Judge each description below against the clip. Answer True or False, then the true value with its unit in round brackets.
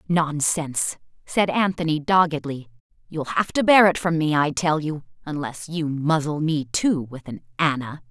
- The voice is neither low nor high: True (155 Hz)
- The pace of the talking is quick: False (155 wpm)